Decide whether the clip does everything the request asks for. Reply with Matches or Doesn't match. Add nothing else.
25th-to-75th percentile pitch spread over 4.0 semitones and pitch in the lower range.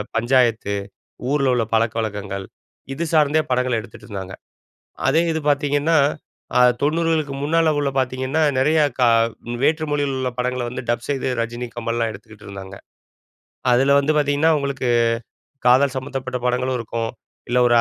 Doesn't match